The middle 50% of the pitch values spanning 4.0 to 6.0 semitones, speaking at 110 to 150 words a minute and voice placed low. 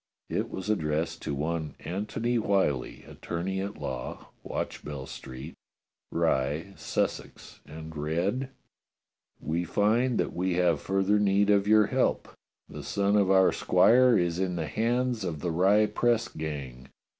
Yes: average, 4.8 semitones; average, 140 wpm; very low, 95 Hz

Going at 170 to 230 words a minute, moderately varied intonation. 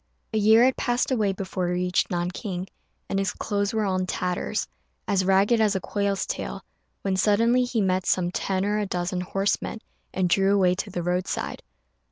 No: average, 190 wpm; narrow, 2.2 semitones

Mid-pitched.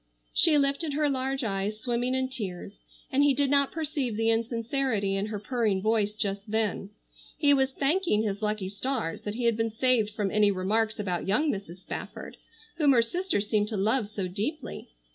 No: high, 225 Hz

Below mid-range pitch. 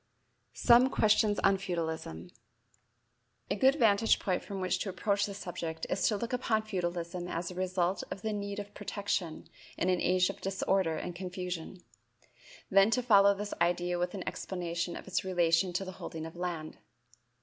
No: medium, 185 Hz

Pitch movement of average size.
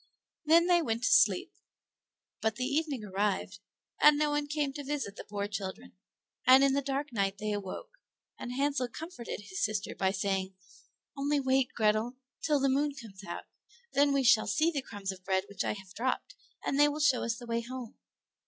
No: wide, 5.9 semitones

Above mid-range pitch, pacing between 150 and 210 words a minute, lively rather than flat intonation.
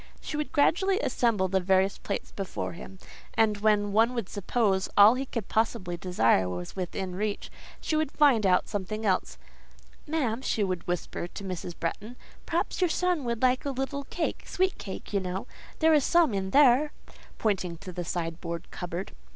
Yes: high, 210 Hz; average, 170 wpm; wide, 6.4 semitones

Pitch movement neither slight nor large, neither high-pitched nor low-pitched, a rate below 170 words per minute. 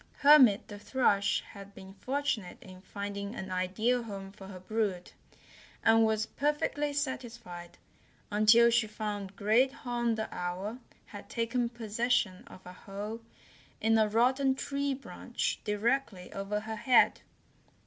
No: average, 3.4 semitones; high, 220 Hz; slow, 135 wpm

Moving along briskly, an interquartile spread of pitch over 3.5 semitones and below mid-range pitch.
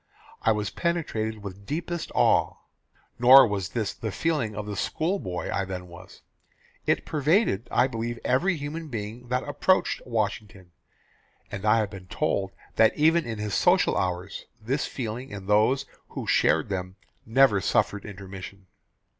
No: average, 155 wpm; wide, 5.4 semitones; low, 110 Hz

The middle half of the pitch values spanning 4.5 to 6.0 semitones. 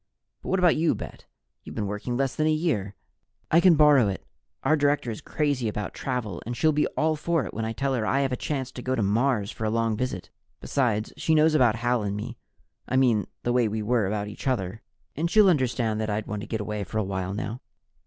Yes: average, 5.1 semitones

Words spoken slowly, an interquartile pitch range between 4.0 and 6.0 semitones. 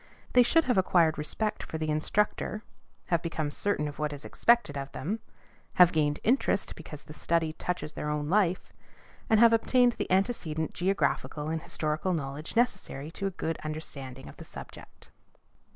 No: average, 170 wpm; average, 5.1 semitones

